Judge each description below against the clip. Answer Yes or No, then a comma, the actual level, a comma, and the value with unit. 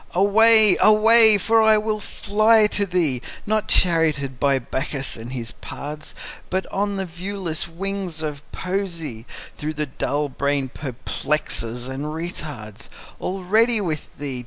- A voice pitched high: No, medium, 170 Hz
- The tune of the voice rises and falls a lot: Yes, wide, 6.2 semitones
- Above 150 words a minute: No, slow, 135 wpm